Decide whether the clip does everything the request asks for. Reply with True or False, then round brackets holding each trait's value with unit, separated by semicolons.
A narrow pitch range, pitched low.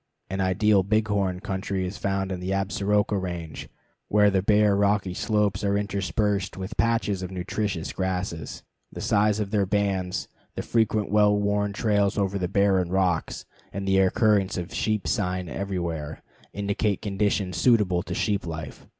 True (1.8 semitones; 100 Hz)